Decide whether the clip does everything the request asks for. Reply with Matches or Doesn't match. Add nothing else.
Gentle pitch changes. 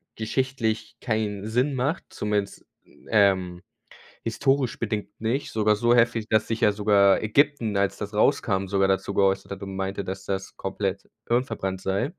Doesn't match